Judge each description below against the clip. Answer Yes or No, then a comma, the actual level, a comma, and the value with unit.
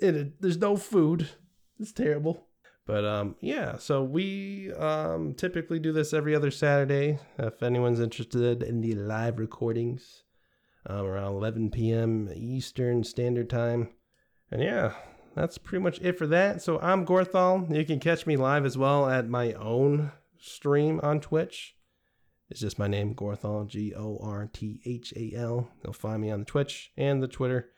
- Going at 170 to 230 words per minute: No, average, 155 wpm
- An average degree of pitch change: No, wide, 5.8 semitones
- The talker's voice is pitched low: Yes, low, 130 Hz